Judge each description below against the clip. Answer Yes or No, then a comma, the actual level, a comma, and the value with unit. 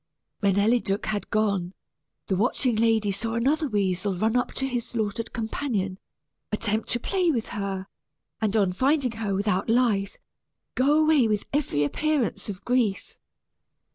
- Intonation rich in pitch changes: No, average, 3.9 semitones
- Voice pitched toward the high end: Yes, high, 220 Hz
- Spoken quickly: No, average, 145 wpm